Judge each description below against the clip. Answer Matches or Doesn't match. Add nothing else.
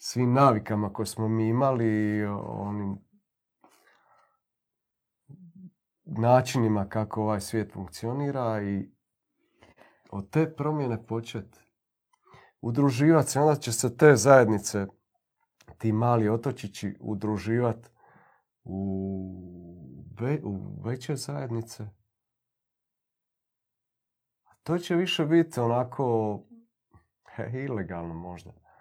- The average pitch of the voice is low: Matches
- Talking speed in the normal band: Doesn't match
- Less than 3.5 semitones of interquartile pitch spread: Doesn't match